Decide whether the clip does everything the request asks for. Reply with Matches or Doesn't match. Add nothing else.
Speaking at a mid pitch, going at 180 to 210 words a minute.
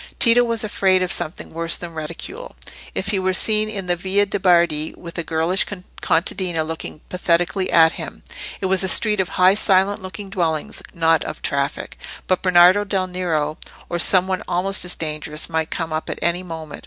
Matches